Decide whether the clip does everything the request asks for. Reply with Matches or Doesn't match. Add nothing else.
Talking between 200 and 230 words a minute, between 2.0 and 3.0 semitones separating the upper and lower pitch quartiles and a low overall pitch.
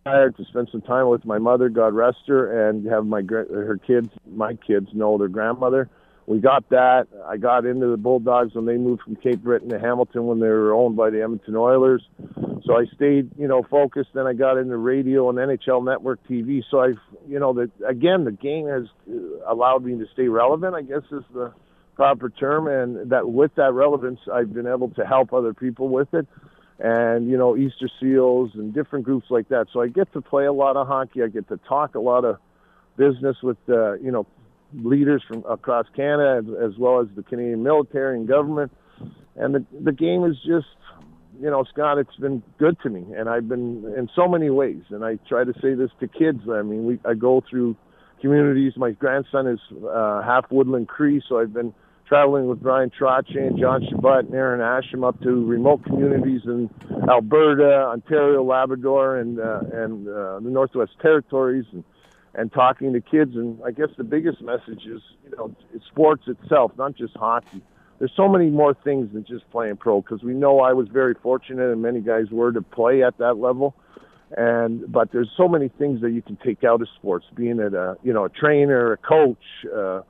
Matches